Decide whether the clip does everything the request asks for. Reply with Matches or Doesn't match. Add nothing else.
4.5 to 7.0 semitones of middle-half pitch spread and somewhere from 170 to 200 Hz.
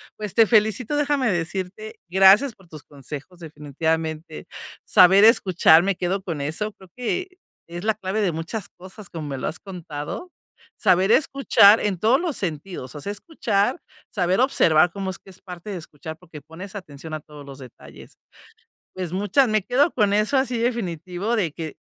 Matches